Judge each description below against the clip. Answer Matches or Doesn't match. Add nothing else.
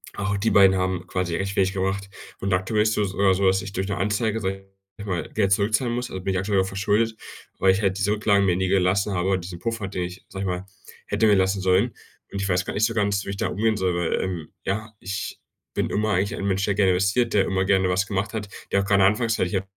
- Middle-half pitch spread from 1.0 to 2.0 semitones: Matches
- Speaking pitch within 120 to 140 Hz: Doesn't match